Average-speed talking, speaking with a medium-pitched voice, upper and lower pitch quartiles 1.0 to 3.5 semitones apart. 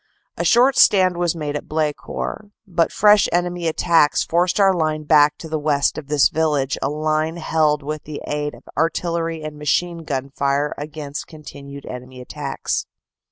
Yes: average, 160 wpm; medium, 155 Hz; narrow, 2.4 semitones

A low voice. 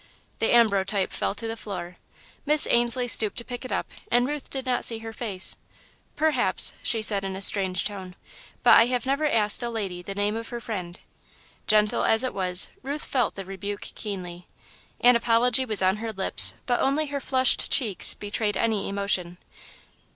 No: high, 220 Hz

